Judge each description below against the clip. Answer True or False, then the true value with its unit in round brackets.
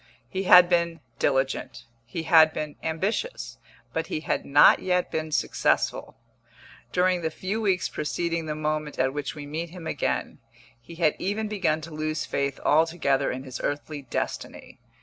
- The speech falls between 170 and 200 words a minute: False (160 wpm)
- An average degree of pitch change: True (3.0 semitones)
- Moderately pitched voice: True (160 Hz)